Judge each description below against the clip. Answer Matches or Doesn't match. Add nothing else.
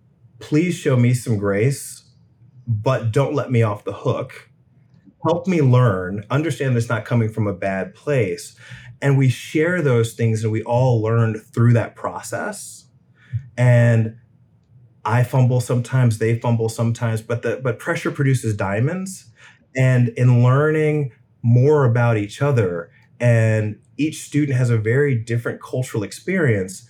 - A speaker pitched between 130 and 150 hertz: Doesn't match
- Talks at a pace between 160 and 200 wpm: Doesn't match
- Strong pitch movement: Doesn't match